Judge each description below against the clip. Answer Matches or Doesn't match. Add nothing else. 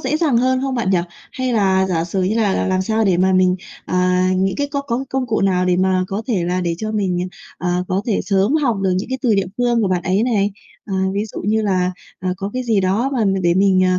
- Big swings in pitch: Doesn't match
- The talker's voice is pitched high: Matches